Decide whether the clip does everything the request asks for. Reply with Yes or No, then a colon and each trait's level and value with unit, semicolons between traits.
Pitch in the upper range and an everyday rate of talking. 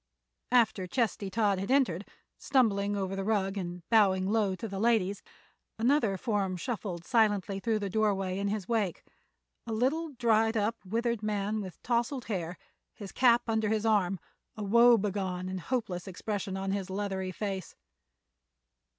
Yes: high, 205 Hz; average, 150 wpm